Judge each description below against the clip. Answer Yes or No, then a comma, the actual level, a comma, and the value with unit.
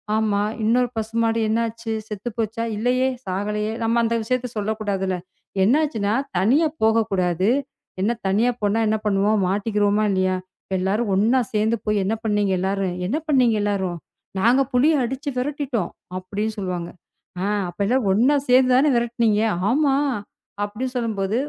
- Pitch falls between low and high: No, high, 220 Hz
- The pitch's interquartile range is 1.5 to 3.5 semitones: Yes, average, 3.2 semitones